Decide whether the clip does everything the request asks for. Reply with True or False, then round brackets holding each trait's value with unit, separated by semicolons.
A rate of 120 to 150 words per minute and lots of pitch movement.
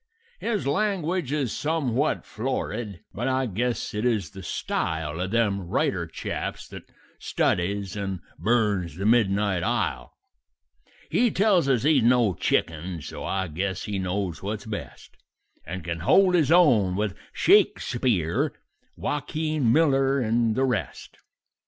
True (135 wpm; 6.1 semitones)